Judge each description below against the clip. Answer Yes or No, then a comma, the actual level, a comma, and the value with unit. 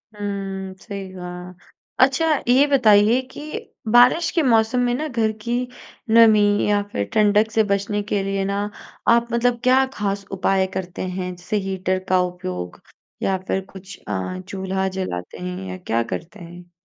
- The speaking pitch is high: Yes, high, 200 Hz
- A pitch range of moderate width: Yes, average, 3.6 semitones